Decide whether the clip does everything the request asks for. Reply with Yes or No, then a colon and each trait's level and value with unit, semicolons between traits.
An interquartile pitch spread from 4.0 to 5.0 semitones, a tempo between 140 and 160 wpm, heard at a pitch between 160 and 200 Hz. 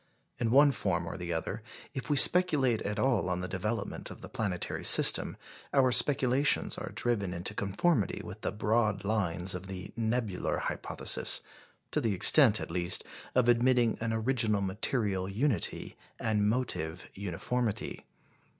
No: average, 4.5 semitones; average, 150 wpm; low, 110 Hz